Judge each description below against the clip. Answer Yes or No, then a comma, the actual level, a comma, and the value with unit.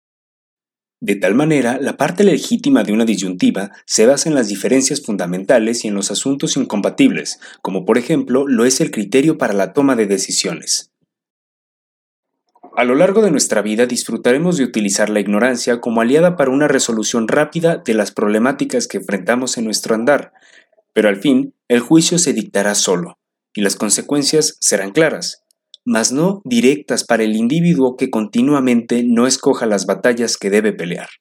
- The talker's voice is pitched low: Yes, low, 125 Hz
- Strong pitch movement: Yes, wide, 5.9 semitones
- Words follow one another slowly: No, average, 165 wpm